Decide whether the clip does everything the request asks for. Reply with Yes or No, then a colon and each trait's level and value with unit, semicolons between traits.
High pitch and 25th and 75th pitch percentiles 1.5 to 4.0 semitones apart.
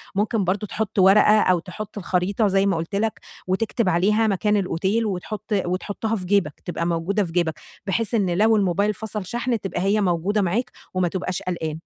Yes: high, 195 Hz; average, 2.9 semitones